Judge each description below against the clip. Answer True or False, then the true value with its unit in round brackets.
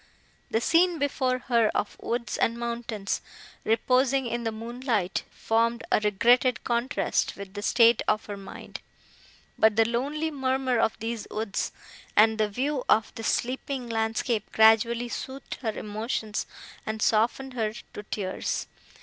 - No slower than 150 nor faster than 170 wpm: False (140 wpm)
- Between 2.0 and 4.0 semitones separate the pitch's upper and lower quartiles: True (2.6 semitones)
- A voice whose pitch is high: True (230 Hz)